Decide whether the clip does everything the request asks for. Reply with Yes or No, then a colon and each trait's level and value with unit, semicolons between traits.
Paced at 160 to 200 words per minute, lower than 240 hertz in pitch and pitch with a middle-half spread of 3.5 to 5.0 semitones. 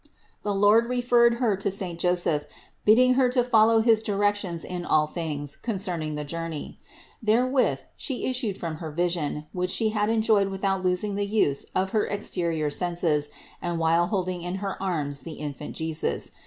Yes: average, 170 wpm; medium, 185 Hz; average, 4.7 semitones